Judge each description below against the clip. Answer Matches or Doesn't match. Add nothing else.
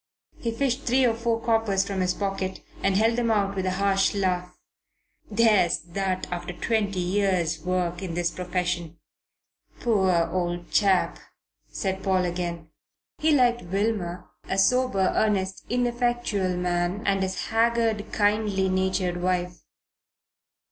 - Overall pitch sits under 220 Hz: Matches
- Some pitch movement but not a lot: Matches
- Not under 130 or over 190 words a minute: Matches